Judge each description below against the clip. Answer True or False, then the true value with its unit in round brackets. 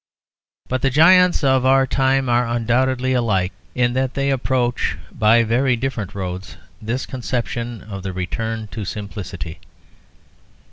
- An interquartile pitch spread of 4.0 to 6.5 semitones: False (3.6 semitones)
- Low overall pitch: True (120 Hz)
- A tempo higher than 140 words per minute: False (135 wpm)